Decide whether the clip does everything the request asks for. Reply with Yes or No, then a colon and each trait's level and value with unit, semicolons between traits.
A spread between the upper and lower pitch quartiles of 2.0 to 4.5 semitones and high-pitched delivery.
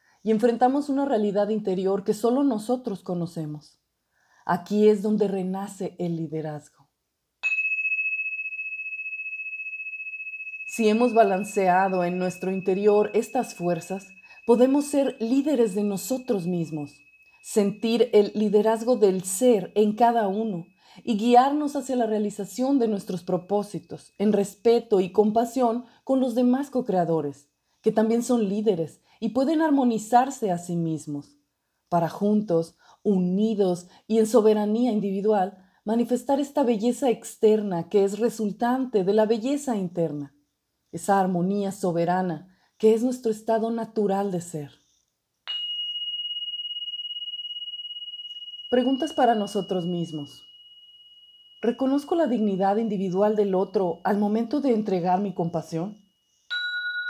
No: average, 5.2 semitones; high, 215 Hz